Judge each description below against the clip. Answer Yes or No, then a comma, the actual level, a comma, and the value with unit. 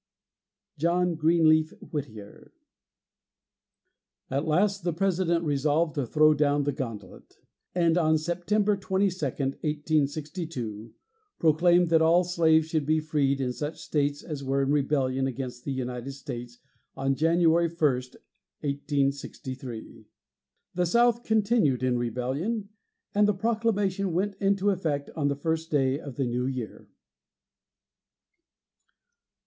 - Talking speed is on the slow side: Yes, slow, 120 wpm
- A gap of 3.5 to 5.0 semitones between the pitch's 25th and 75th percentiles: Yes, average, 4.2 semitones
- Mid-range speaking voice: Yes, medium, 155 Hz